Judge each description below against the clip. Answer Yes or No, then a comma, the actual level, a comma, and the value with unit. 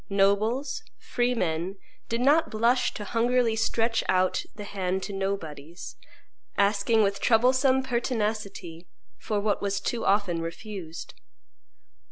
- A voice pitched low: No, high, 210 Hz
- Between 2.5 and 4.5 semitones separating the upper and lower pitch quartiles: Yes, average, 3.5 semitones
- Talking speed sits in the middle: No, slow, 120 wpm